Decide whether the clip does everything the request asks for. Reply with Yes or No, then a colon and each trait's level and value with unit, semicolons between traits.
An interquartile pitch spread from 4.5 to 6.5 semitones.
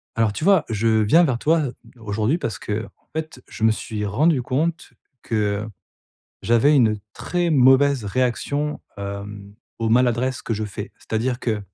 Yes: average, 4.9 semitones